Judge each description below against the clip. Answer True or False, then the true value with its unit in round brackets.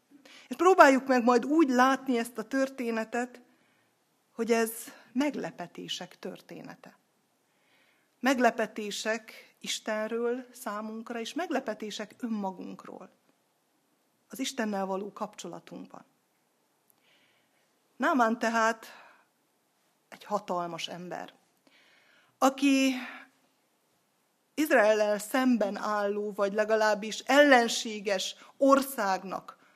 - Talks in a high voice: True (230 Hz)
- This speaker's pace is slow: True (75 wpm)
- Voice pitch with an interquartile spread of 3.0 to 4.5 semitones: True (3.8 semitones)